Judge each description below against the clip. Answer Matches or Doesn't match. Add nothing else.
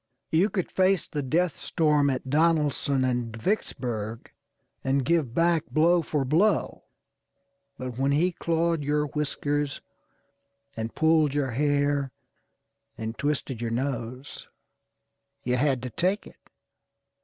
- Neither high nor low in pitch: Matches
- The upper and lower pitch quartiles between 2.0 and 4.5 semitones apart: Matches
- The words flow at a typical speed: Doesn't match